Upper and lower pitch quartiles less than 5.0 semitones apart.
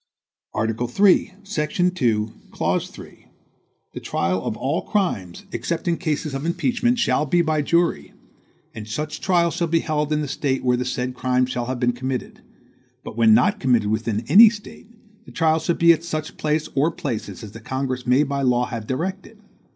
No: wide, 5.6 semitones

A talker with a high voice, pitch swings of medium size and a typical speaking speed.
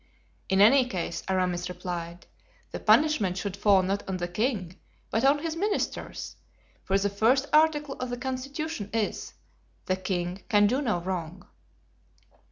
No: high, 200 Hz; wide, 6.3 semitones; average, 150 wpm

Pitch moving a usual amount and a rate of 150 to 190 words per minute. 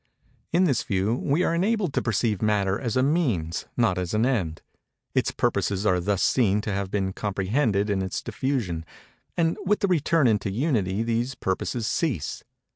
No: wide, 6.0 semitones; average, 170 wpm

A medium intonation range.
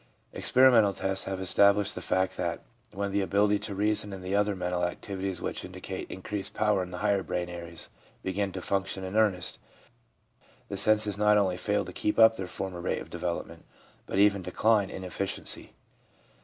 No: narrow, 2.0 semitones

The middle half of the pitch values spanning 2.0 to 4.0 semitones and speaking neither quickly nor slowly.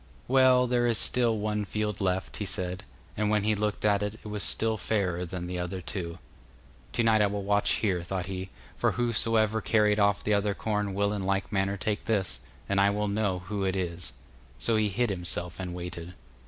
No: narrow, 2.4 semitones; fast, 210 wpm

